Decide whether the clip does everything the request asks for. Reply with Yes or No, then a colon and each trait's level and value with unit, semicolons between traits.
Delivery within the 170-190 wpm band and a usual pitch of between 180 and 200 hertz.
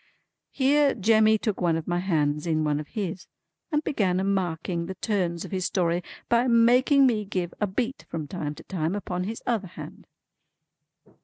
Yes: average, 180 wpm; high, 190 Hz